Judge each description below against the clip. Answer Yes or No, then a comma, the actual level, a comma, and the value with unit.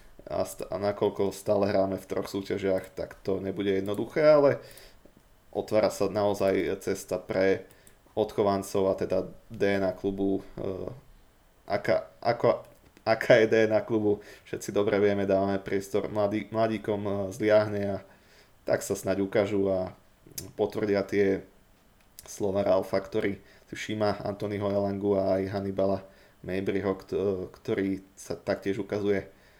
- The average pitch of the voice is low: Yes, low, 100 Hz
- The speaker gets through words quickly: No, average, 120 wpm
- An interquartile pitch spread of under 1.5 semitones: Yes, narrow, 1.1 semitones